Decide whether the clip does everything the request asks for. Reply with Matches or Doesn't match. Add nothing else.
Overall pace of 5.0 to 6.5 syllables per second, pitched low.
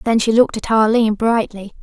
Doesn't match